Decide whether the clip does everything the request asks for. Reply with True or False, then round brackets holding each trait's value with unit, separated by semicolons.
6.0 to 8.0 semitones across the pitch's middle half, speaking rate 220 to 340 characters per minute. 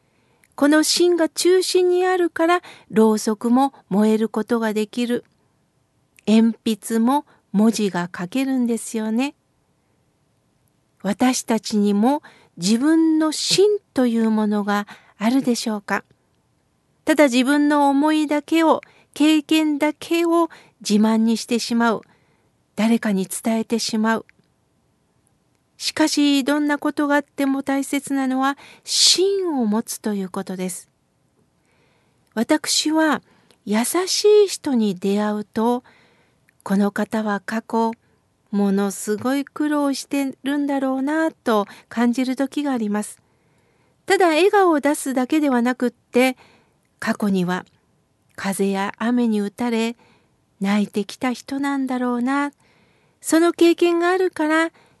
False (5.5 semitones; 230 characters per minute)